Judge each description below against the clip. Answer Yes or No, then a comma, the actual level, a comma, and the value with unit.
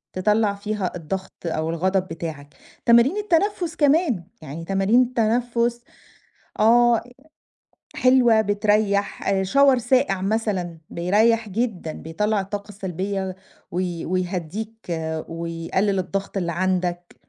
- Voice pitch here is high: Yes, high, 200 Hz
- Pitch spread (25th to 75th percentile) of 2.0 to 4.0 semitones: No, average, 4.4 semitones